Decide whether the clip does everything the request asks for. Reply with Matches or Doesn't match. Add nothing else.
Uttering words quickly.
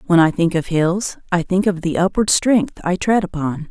Matches